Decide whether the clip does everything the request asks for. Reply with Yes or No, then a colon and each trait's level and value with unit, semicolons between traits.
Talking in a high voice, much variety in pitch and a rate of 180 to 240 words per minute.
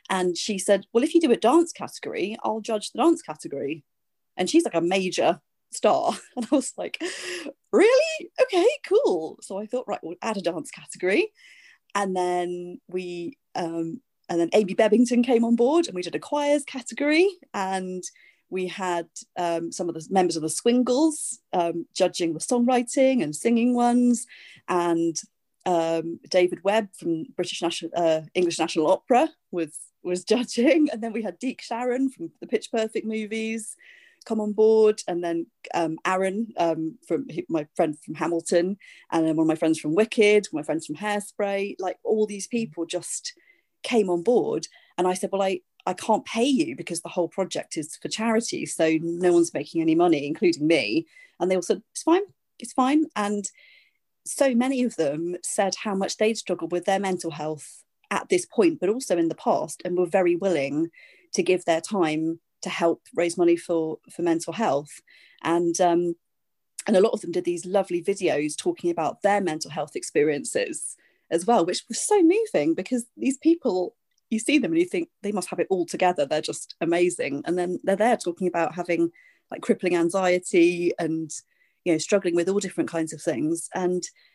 Yes: high, 195 Hz; wide, 6.3 semitones; average, 190 wpm